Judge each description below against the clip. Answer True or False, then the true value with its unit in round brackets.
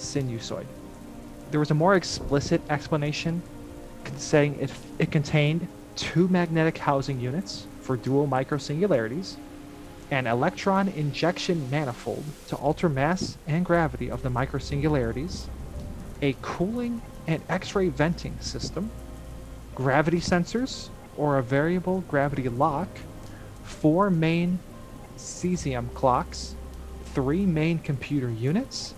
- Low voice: False (150 Hz)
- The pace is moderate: False (110 wpm)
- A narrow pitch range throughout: False (4.5 semitones)